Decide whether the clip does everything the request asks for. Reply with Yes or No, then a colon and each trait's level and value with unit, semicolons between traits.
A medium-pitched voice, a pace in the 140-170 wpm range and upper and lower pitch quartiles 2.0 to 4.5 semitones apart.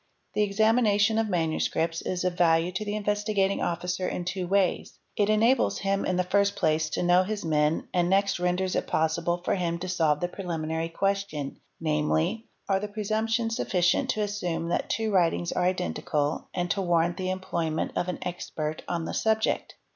No: medium, 180 Hz; average, 190 wpm; average, 3.3 semitones